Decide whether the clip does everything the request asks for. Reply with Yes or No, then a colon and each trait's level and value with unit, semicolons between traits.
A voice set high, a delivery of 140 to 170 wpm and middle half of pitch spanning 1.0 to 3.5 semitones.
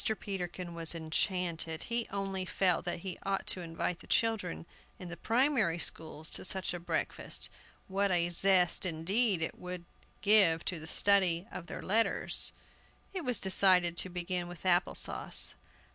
No: medium, 180 Hz; average, 160 wpm; narrow, 2.5 semitones